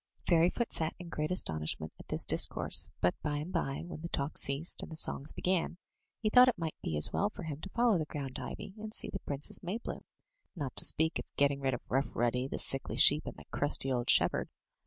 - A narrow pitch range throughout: No, average, 4.6 semitones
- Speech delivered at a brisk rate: Yes, fast, 225 wpm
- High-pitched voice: No, medium, 155 Hz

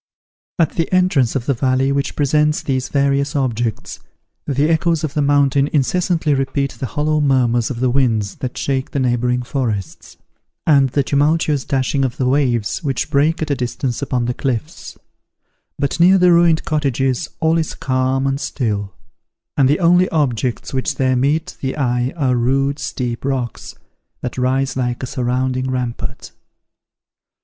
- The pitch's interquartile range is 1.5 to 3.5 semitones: Yes, average, 2.8 semitones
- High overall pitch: No, low, 135 Hz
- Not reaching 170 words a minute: Yes, average, 160 wpm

